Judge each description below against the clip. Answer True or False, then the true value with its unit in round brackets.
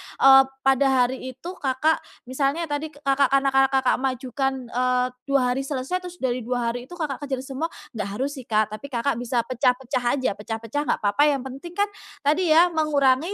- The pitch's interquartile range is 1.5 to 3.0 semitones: True (2.5 semitones)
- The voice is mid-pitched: False (265 Hz)